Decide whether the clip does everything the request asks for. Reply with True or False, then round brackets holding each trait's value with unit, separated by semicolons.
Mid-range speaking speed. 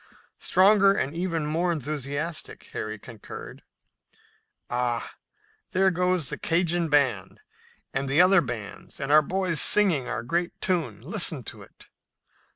False (130 wpm)